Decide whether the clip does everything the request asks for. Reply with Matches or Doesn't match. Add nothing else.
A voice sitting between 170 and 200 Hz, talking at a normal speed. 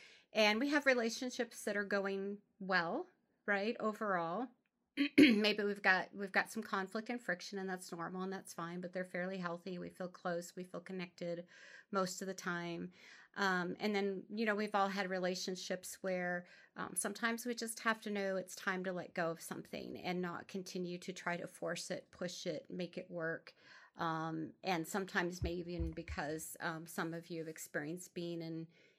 Matches